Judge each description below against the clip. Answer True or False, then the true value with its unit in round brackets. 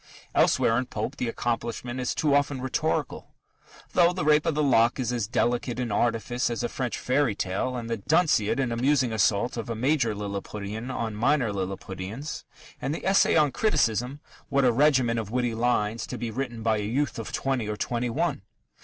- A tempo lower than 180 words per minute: False (190 wpm)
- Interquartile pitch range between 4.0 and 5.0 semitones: False (3.4 semitones)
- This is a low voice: True (120 Hz)